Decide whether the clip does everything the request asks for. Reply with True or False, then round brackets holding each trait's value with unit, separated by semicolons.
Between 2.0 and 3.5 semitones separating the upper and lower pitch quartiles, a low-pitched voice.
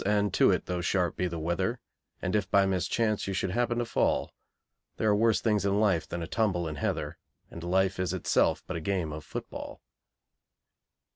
True (3.2 semitones; 95 Hz)